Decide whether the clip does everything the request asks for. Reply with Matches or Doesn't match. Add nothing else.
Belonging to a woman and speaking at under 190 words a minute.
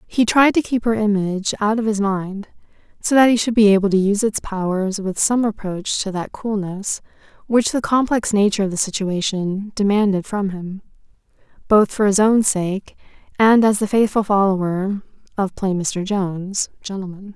Matches